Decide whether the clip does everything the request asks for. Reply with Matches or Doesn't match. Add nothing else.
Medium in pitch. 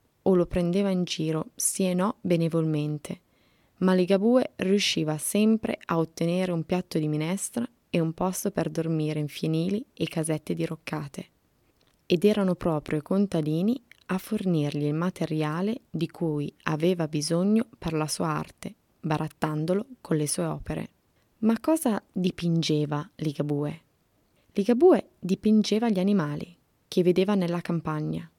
Matches